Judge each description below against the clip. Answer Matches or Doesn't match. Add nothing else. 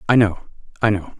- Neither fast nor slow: Matches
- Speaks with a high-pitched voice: Doesn't match